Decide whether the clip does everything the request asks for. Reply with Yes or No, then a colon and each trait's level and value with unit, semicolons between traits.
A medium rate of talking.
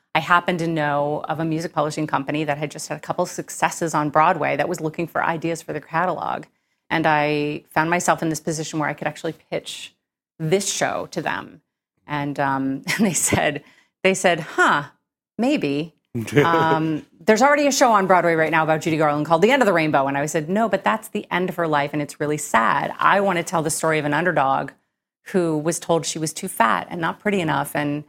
No: fast, 225 wpm